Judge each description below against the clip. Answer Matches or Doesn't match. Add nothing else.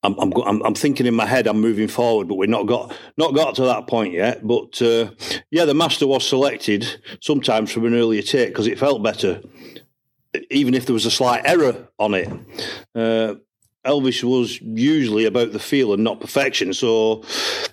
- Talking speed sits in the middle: Matches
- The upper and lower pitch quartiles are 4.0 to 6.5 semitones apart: Doesn't match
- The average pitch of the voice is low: Matches